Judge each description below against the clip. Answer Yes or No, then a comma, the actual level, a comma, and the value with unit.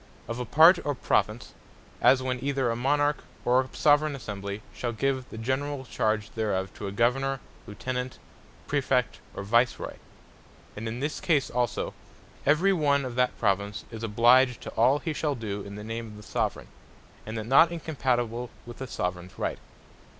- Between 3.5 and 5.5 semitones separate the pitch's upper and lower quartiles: Yes, average, 3.8 semitones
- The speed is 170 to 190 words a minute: Yes, average, 175 wpm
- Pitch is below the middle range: Yes, low, 125 Hz